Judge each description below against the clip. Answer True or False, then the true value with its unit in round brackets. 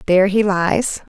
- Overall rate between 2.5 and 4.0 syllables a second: False (4.5 syllables/s)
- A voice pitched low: False (195 Hz)